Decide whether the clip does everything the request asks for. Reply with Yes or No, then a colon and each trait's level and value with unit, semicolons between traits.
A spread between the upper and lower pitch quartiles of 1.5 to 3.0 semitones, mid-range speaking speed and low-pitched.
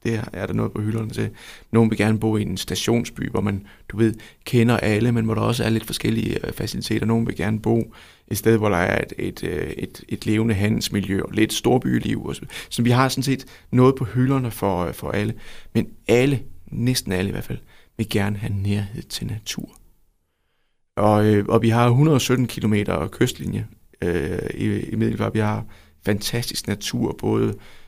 Yes: narrow, 2.4 semitones; average, 190 wpm; low, 110 Hz